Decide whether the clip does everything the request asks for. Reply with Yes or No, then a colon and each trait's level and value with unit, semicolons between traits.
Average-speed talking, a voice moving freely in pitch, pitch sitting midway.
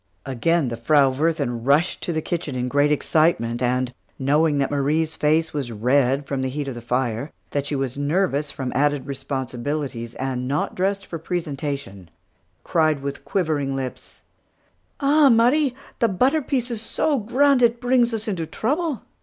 Yes: average, 160 wpm; wide, 6.0 semitones; medium, 145 Hz